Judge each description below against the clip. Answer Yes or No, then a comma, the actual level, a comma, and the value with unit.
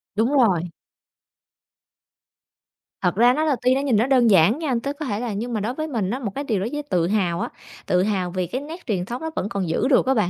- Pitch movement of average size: No, wide, 6.0 semitones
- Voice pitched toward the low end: No, high, 230 Hz